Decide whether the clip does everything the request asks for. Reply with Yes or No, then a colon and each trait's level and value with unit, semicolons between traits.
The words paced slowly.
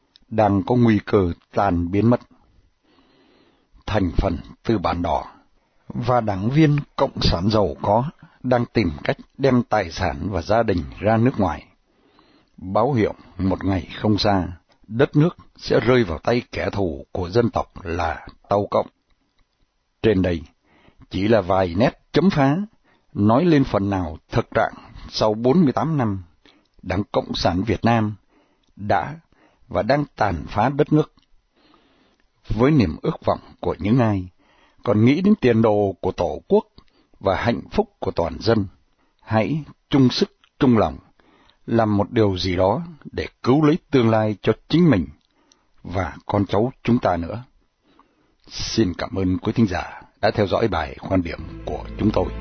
Yes: slow, 160 wpm